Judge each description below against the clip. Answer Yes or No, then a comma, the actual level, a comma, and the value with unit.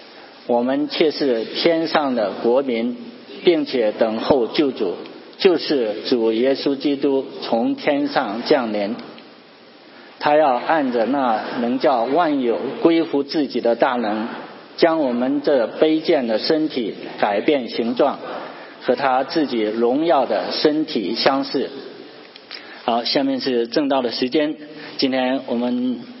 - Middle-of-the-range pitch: Yes, medium, 145 Hz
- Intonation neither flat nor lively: Yes, average, 3.7 semitones